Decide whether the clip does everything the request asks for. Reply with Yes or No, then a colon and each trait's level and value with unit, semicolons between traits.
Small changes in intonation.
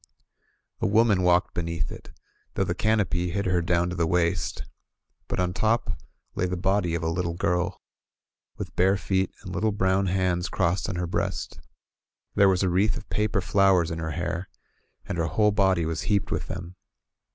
Yes: narrow, 2.3 semitones